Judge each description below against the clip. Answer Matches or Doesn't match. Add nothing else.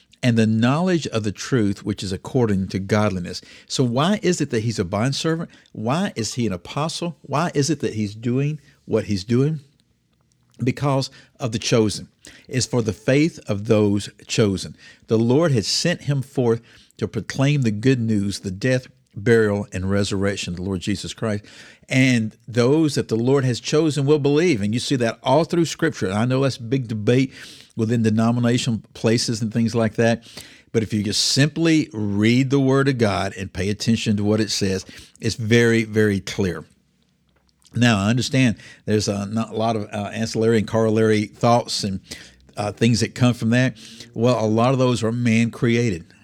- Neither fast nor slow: Matches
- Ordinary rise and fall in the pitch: Matches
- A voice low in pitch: Matches